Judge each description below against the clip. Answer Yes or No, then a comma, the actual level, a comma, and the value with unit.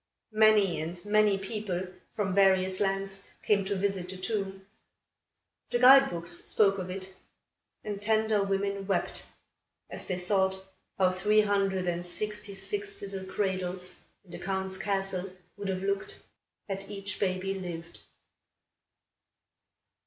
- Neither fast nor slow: No, slow, 130 wpm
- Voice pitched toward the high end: Yes, high, 195 Hz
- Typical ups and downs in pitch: No, narrow, 1.5 semitones